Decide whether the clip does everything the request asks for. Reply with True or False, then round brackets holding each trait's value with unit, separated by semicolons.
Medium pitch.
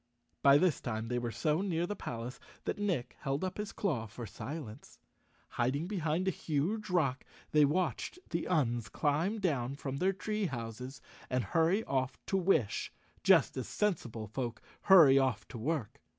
True (145 Hz)